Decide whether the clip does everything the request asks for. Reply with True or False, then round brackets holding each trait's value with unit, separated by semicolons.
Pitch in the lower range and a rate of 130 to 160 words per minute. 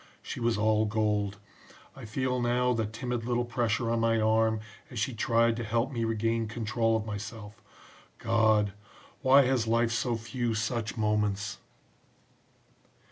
True (115 Hz; 145 wpm)